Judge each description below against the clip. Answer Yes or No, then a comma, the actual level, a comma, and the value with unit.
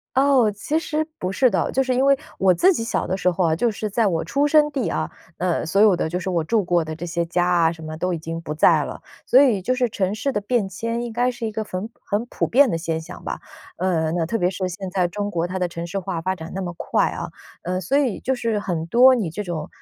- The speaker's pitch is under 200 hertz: Yes, high, 190 Hz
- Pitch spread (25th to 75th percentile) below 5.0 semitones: No, wide, 5.4 semitones